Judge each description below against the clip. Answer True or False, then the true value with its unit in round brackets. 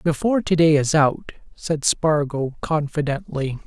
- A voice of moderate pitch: True (150 Hz)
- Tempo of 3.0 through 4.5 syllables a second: True (4.2 syllables/s)